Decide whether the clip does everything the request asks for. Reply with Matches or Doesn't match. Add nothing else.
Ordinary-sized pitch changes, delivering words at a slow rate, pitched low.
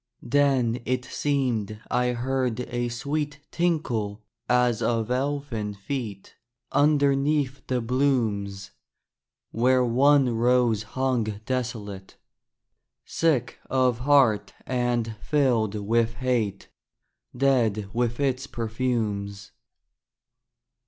Matches